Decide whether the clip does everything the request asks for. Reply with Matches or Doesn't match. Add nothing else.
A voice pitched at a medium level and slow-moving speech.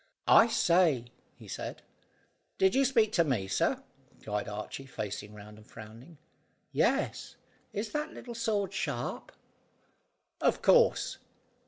Matches